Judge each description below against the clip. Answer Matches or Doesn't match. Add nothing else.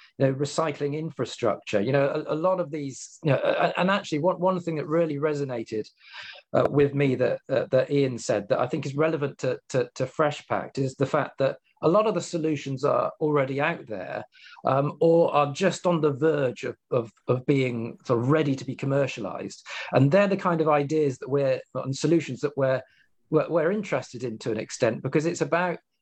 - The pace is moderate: Doesn't match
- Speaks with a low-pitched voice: Doesn't match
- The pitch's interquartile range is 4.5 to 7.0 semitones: Doesn't match